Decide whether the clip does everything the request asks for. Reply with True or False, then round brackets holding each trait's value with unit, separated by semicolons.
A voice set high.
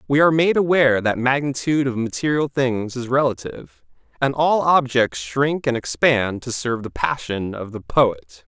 False (130 Hz)